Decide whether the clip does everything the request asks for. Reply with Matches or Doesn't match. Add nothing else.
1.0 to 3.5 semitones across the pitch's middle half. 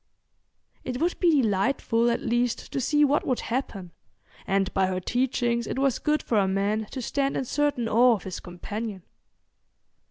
Doesn't match